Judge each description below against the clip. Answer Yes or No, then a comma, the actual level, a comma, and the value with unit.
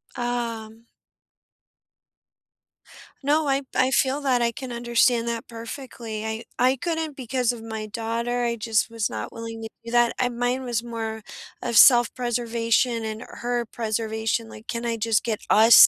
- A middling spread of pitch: No, narrow, 1.5 semitones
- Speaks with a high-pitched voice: Yes, high, 235 Hz